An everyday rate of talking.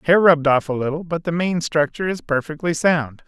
No: fast, 220 wpm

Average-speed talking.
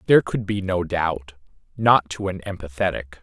Yes: average, 170 wpm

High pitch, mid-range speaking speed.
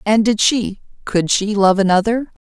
Yes: high, 210 Hz; average, 170 wpm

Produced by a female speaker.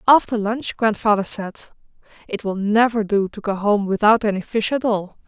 Yes: female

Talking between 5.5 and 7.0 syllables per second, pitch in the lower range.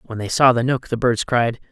No: 5.0 syllables/s; low, 120 Hz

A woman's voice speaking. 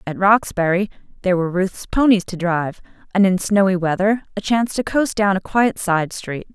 Yes: female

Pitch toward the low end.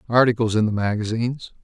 Yes: low, 115 Hz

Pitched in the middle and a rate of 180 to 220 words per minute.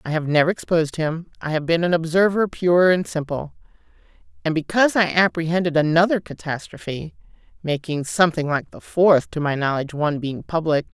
No: medium, 165 Hz; average, 160 wpm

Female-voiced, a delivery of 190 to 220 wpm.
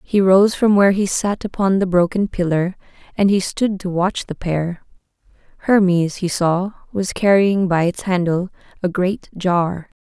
No: female; average, 170 wpm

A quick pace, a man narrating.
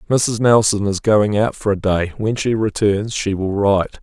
Yes: fast, 210 wpm; male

